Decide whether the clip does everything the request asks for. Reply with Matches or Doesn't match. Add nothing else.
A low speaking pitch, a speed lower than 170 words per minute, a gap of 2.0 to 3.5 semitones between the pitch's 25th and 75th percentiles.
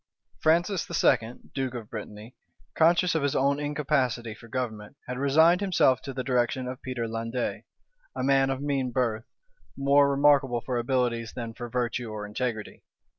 Matches